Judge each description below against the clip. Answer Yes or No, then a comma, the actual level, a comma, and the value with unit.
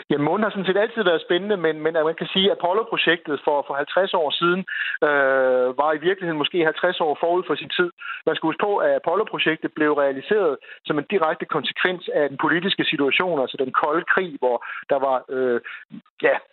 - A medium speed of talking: Yes, average, 205 wpm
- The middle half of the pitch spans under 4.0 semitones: No, average, 4.8 semitones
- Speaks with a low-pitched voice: No, medium, 160 Hz